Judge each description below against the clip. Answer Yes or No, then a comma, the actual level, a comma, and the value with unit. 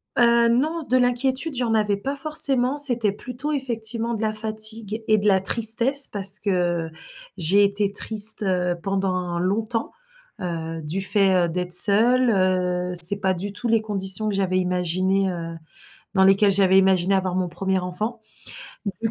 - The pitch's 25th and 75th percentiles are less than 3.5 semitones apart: No, average, 3.8 semitones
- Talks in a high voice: Yes, high, 200 Hz